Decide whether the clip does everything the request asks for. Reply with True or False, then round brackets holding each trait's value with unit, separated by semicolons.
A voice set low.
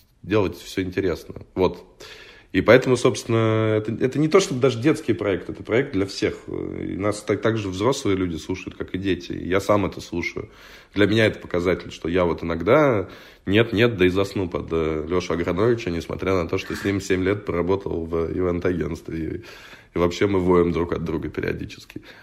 True (95 Hz)